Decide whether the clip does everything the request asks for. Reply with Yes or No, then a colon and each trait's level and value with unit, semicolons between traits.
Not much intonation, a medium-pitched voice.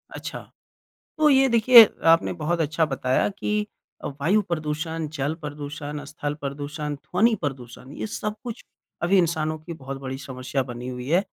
No: average, 3.9 semitones; medium, 155 Hz